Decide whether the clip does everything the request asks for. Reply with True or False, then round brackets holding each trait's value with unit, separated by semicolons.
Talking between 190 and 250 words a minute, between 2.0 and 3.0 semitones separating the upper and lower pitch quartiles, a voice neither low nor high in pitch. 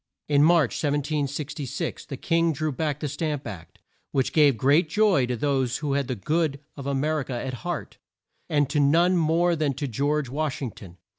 True (200 wpm; 2.7 semitones; 145 Hz)